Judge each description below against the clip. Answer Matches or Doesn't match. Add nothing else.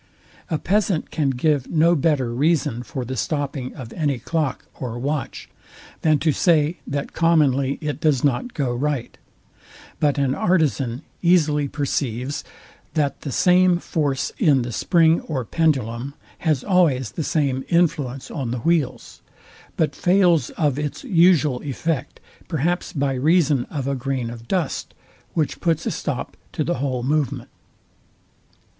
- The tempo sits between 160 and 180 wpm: Doesn't match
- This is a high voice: Doesn't match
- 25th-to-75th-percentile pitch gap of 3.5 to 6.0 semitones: Matches